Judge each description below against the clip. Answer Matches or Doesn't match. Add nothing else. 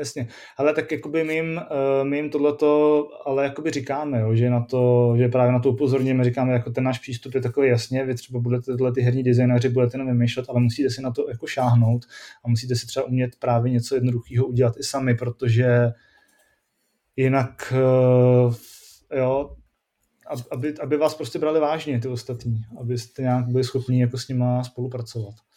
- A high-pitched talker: Doesn't match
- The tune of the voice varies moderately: Doesn't match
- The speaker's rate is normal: Doesn't match